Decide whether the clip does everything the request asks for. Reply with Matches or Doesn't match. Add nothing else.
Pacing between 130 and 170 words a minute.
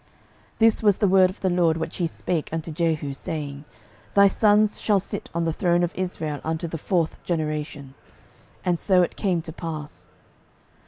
Doesn't match